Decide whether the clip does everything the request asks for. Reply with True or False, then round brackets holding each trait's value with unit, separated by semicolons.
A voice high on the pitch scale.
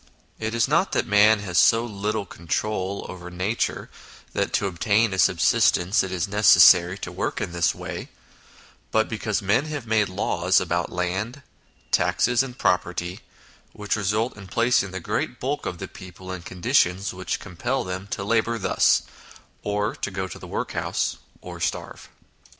False (100 Hz)